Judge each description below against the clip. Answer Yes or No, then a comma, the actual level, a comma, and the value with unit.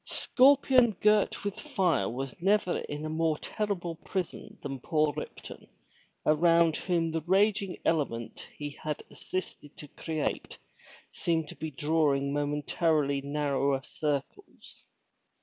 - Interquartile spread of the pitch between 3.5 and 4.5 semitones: Yes, average, 3.9 semitones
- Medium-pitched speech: Yes, medium, 160 Hz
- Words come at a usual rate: No, slow, 120 wpm